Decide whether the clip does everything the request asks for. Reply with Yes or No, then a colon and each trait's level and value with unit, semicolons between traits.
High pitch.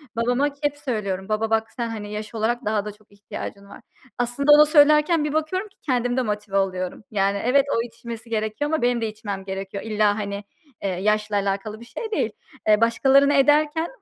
Yes: high, 225 Hz